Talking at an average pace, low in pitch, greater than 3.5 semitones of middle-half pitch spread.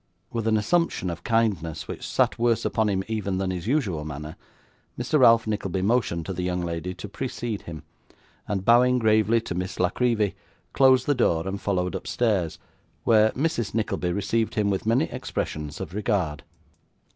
Yes: average, 170 wpm; low, 105 Hz; average, 4.3 semitones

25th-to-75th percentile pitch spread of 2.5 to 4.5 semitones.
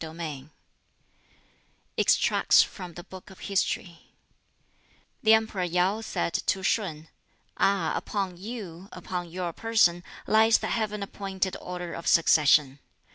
Yes: average, 3.1 semitones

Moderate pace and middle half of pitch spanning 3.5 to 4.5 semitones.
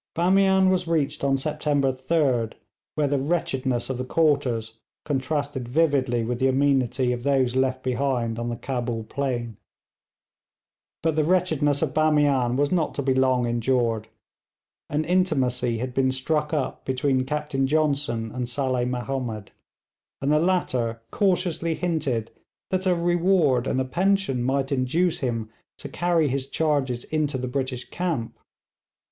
Yes: average, 145 wpm; average, 3.8 semitones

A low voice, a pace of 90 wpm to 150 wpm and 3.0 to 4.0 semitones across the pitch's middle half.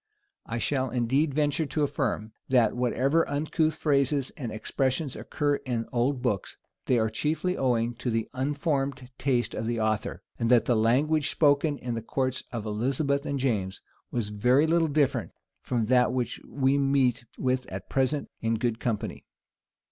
No: low, 130 Hz; average, 165 wpm; average, 3.4 semitones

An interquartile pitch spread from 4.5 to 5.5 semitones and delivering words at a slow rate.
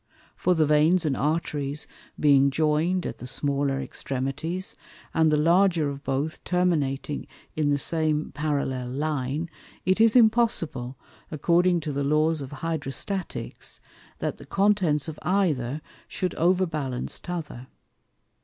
No: average, 3.8 semitones; slow, 125 wpm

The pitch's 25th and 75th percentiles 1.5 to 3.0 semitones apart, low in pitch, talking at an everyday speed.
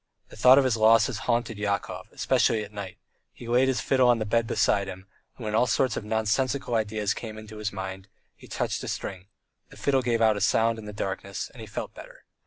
No: average, 2.7 semitones; low, 110 Hz; fast, 225 wpm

